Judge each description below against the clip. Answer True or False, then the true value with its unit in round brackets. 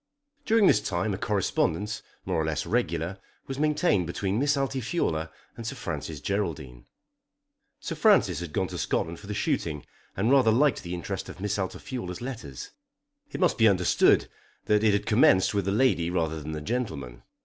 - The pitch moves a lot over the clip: True (6.4 semitones)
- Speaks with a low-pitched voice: True (100 Hz)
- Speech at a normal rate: True (175 wpm)